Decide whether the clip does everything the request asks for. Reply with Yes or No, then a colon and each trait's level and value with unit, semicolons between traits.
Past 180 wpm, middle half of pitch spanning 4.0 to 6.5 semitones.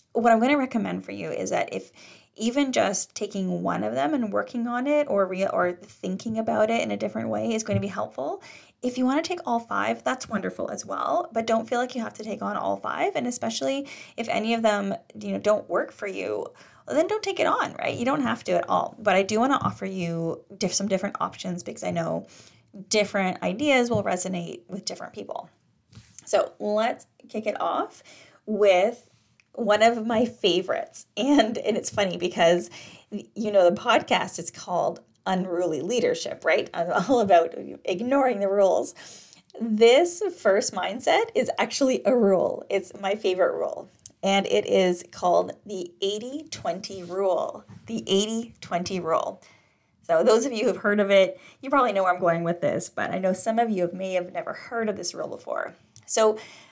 Yes: average, 200 wpm; average, 4.4 semitones